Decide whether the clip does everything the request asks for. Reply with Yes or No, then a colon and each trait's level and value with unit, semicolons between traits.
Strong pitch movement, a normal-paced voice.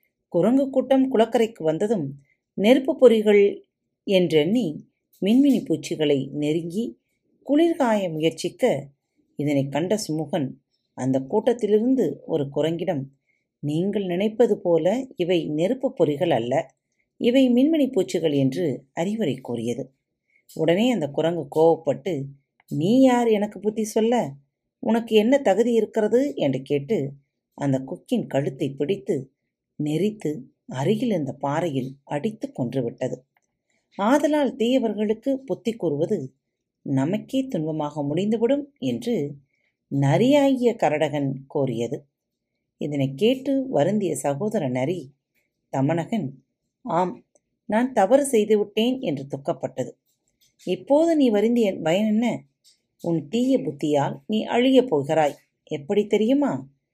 Yes: wide, 8.3 semitones; average, 100 wpm